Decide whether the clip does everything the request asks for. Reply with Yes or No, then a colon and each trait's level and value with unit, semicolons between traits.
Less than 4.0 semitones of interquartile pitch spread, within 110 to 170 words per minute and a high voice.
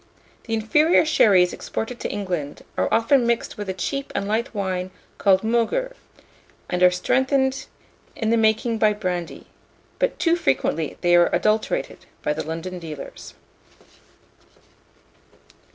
No: average, 4.8 semitones; slow, 135 wpm; high, 215 Hz